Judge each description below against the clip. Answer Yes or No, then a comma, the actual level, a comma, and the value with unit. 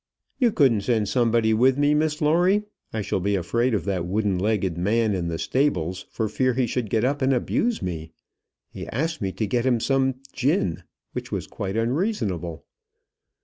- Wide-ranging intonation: Yes, wide, 5.7 semitones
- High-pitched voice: No, low, 115 Hz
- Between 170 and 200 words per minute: Yes, average, 185 wpm